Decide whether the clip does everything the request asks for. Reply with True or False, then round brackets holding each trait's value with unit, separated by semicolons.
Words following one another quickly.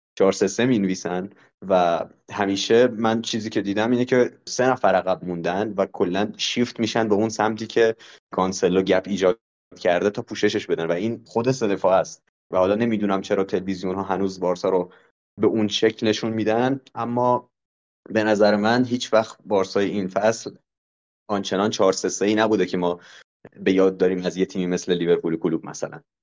True (180 wpm)